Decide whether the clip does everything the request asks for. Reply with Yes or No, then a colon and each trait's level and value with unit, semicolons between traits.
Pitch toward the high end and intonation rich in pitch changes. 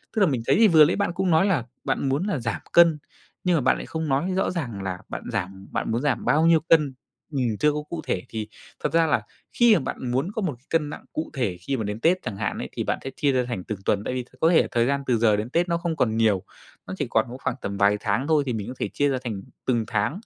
No: low, 135 Hz; wide, 6.6 semitones